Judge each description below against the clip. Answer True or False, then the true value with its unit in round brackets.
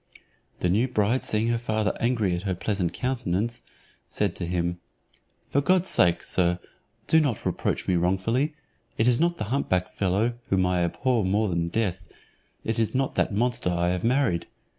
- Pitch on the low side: True (105 Hz)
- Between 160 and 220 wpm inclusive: True (180 wpm)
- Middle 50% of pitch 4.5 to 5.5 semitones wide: True (5.1 semitones)